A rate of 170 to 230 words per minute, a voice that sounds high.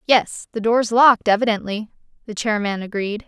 No: average, 145 wpm; high, 220 Hz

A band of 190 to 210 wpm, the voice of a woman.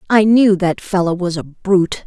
Yes: fast, 205 wpm; female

